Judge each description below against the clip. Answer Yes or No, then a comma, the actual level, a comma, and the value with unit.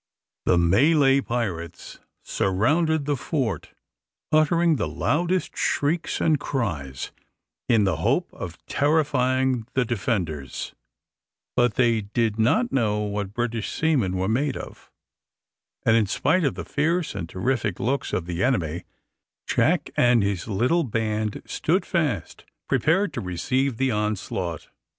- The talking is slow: Yes, slow, 130 wpm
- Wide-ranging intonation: Yes, wide, 6.4 semitones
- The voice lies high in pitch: No, low, 120 Hz